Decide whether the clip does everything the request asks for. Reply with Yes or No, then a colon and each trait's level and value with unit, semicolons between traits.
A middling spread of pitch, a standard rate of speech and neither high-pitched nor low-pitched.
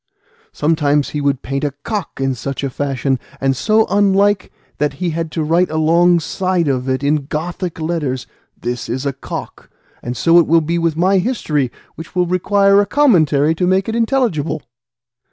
Yes: average, 4.5 semitones; average, 175 wpm; medium, 160 Hz